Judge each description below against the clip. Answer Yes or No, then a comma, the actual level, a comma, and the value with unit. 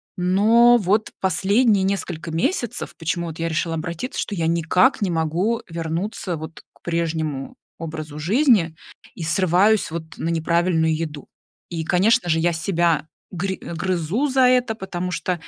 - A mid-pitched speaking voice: Yes, medium, 175 Hz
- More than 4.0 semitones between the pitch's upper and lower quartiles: No, average, 3.6 semitones